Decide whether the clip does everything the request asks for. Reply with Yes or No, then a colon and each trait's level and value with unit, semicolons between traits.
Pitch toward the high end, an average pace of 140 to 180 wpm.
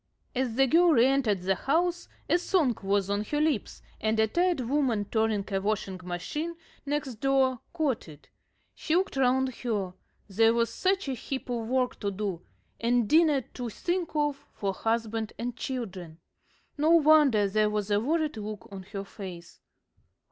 Yes: high, 235 Hz; average, 170 wpm